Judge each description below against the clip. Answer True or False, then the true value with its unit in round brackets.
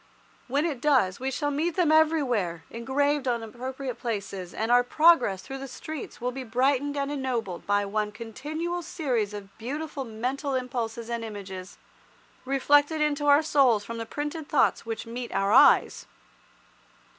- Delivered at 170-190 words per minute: False (155 wpm)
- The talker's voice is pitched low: False (255 Hz)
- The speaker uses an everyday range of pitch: True (4.5 semitones)